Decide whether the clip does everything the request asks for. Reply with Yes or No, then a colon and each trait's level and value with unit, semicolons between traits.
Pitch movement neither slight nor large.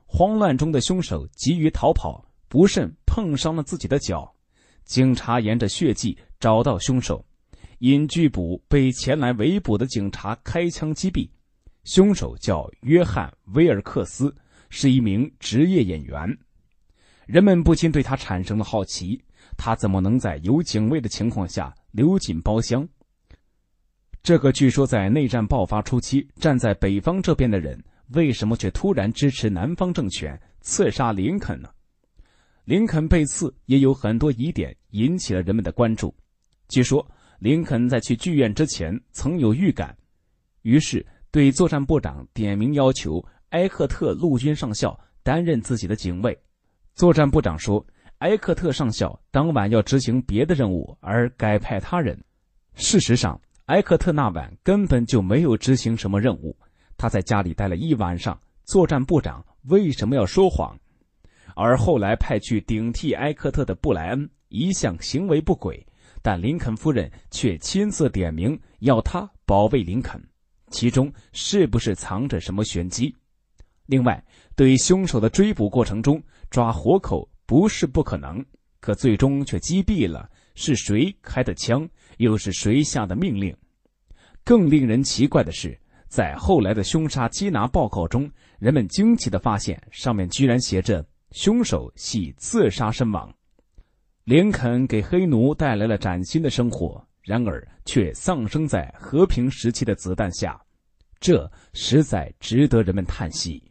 No: wide, 6.4 semitones